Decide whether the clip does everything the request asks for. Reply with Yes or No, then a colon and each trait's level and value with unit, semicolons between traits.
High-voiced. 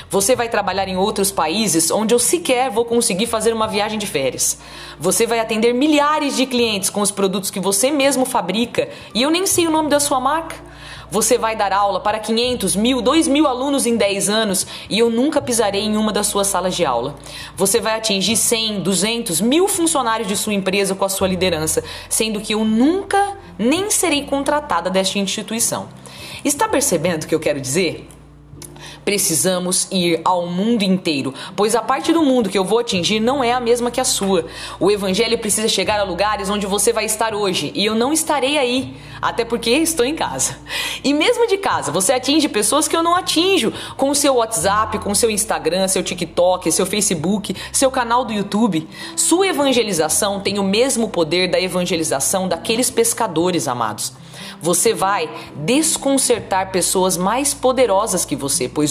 Yes: high, 215 Hz